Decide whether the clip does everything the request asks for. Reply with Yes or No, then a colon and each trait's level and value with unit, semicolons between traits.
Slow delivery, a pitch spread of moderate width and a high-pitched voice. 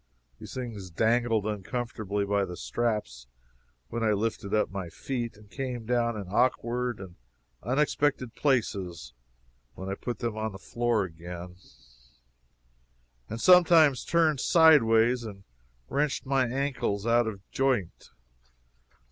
No: slow, 125 wpm; average, 4.0 semitones; low, 115 Hz